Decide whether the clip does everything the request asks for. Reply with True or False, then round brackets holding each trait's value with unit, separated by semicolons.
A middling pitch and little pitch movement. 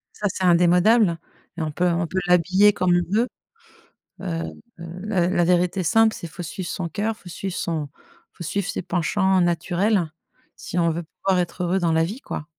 True (180 Hz; 2.1 semitones)